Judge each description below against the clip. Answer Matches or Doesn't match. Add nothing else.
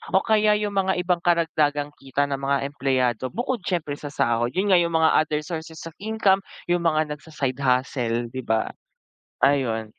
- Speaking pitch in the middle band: Matches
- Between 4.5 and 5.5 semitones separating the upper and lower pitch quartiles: Matches